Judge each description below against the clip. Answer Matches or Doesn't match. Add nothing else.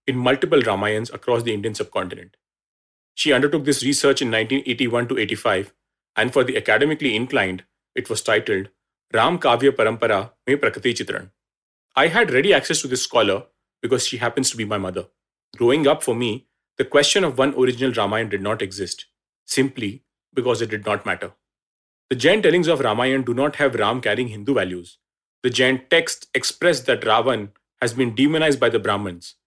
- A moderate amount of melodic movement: Matches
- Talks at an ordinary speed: Matches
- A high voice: Doesn't match